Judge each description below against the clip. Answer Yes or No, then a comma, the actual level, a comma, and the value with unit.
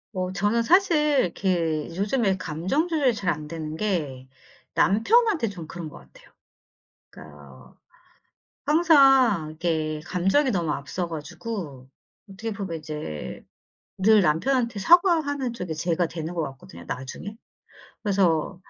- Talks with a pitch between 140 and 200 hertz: Yes, medium, 185 Hz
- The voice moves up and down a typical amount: No, wide, 7.0 semitones